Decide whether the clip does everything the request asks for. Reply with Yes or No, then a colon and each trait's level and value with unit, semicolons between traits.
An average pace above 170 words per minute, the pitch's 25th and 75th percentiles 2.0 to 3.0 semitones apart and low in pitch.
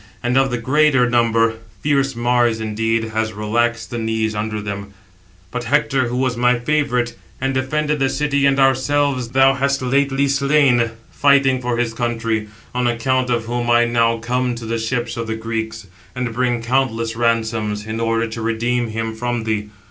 Yes: average, 180 wpm; narrow, 2.6 semitones; low, 120 Hz